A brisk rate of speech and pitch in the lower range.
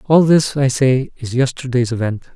No: average, 180 wpm; low, 130 Hz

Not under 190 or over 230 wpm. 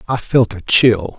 Yes: average, 200 wpm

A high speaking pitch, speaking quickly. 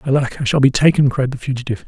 No: low, 130 Hz; fast, 255 wpm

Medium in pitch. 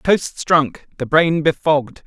Yes: medium, 155 Hz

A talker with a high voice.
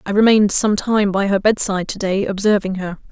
Yes: high, 200 Hz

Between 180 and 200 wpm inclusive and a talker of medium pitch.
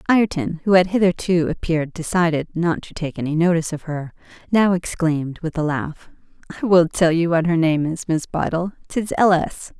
Yes: average, 190 wpm; medium, 170 Hz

